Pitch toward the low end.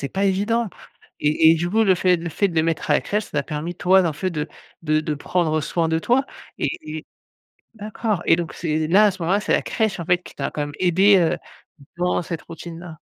No: medium, 175 Hz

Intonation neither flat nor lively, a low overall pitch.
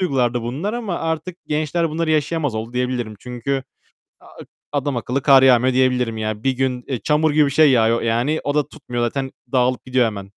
Yes: average, 3.7 semitones; low, 130 Hz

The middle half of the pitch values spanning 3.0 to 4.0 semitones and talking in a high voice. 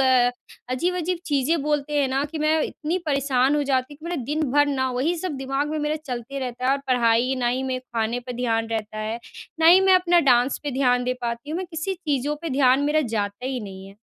Yes: average, 3.4 semitones; very high, 270 Hz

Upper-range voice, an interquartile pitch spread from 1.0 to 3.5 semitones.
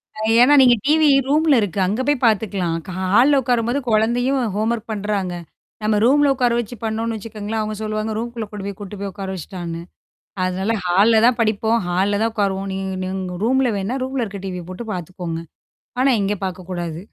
No: high, 215 Hz; average, 3.9 semitones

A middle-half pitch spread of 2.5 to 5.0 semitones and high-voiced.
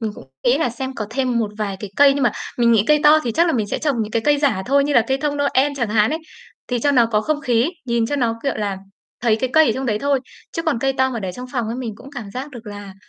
Yes: average, 4.1 semitones; high, 245 Hz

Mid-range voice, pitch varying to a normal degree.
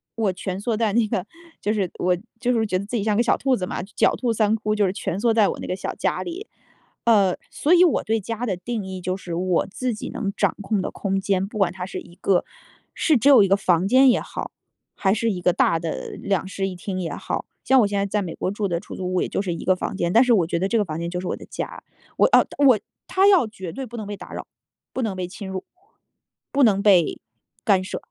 No: high, 200 Hz; average, 3.4 semitones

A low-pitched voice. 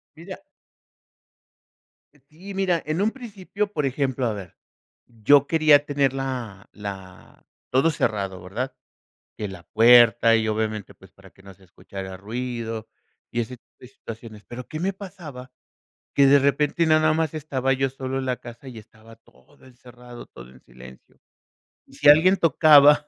Yes: low, 130 Hz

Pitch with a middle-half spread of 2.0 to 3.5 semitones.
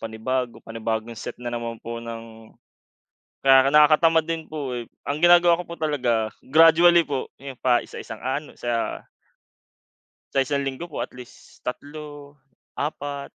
No: average, 4.5 semitones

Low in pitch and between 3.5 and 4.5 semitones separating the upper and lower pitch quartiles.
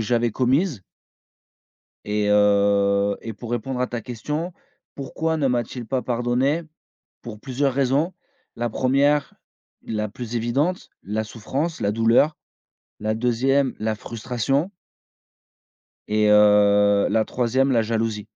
Yes: low, 120 Hz; average, 4.0 semitones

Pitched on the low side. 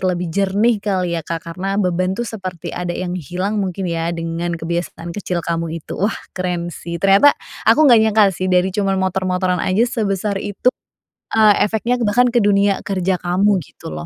No: medium, 185 Hz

